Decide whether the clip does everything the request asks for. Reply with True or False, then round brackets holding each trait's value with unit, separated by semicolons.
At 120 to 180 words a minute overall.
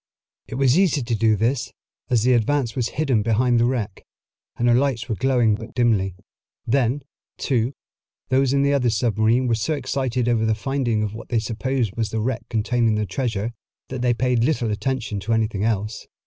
False (190 wpm)